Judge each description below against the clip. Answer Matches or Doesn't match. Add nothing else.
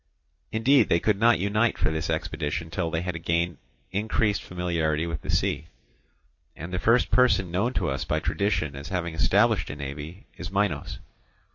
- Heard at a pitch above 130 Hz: Doesn't match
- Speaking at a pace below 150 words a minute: Doesn't match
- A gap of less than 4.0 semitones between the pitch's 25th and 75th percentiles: Doesn't match